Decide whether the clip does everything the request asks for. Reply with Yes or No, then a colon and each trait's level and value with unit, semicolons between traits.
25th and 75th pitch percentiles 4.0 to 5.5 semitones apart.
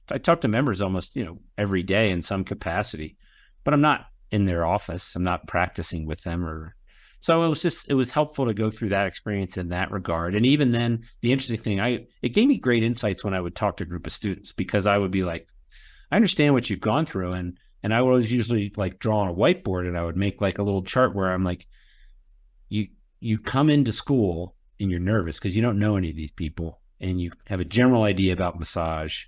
Yes: average, 4.6 semitones